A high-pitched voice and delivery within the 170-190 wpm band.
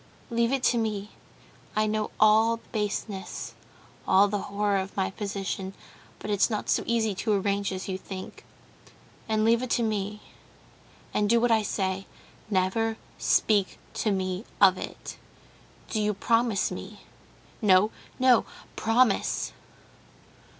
No: high, 210 Hz; average, 140 wpm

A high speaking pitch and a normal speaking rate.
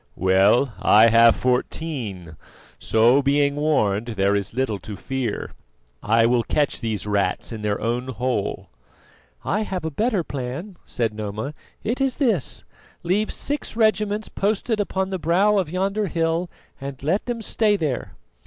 No: medium, 140 Hz; average, 150 wpm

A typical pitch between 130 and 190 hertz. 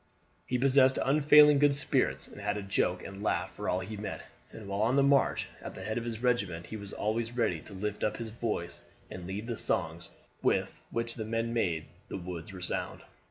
No: low, 110 Hz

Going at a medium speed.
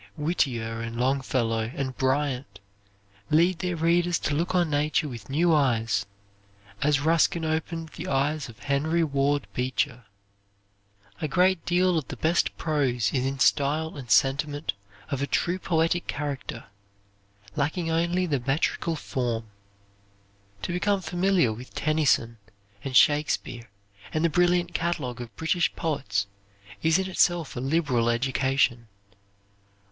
No: slow, 130 wpm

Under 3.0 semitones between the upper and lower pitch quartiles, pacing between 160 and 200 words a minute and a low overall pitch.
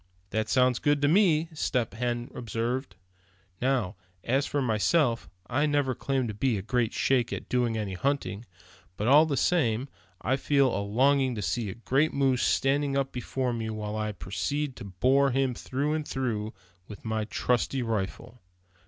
No: average, 3.8 semitones; average, 170 wpm; low, 125 Hz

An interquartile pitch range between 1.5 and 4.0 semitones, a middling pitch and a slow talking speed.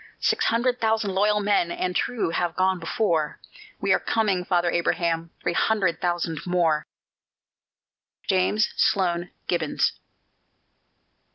Yes: average, 3.5 semitones; medium, 180 Hz; slow, 115 wpm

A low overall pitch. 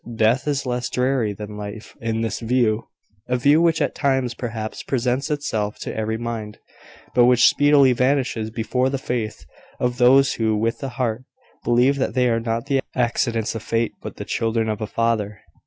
Yes: low, 120 Hz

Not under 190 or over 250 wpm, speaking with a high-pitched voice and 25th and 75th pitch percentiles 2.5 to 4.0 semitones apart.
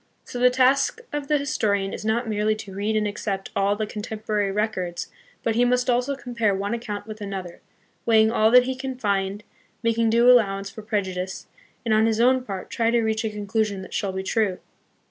Yes: fast, 205 wpm; high, 220 Hz; average, 3.0 semitones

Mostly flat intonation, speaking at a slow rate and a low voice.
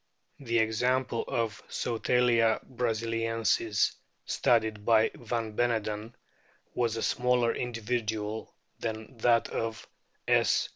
Yes: narrow, 1.5 semitones; slow, 95 wpm; low, 115 Hz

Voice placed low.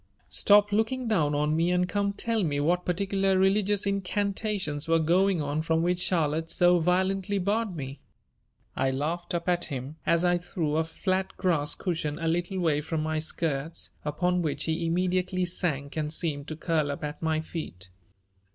No: medium, 170 Hz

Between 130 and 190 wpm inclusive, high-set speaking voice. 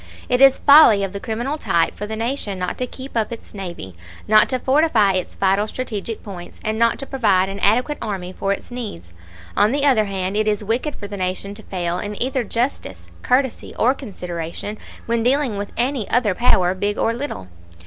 No: average, 200 wpm; high, 215 Hz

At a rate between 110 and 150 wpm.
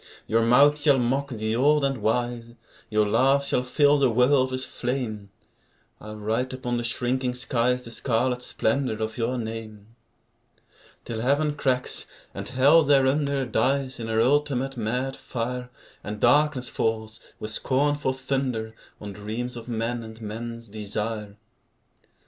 Yes: average, 145 wpm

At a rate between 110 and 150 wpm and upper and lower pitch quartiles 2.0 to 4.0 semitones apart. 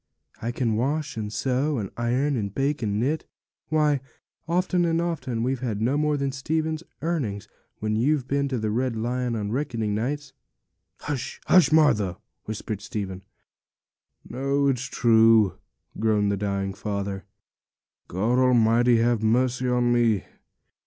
No: average, 145 wpm; average, 4.5 semitones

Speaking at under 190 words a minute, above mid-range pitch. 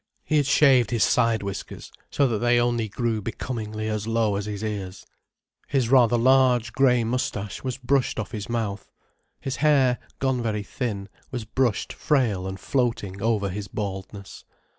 No: average, 160 wpm; low, 115 Hz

